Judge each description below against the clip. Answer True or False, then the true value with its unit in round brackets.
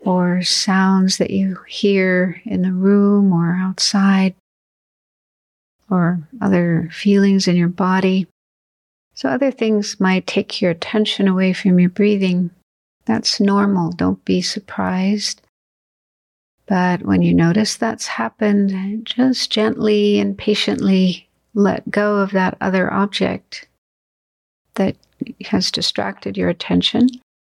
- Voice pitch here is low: False (190 Hz)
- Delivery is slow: True (115 wpm)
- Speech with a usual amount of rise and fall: False (2.2 semitones)